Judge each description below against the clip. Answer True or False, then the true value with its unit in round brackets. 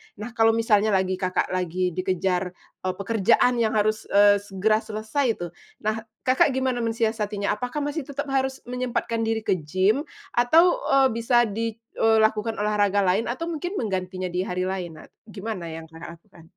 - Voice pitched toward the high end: True (215 Hz)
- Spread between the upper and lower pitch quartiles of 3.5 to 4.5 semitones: True (4.2 semitones)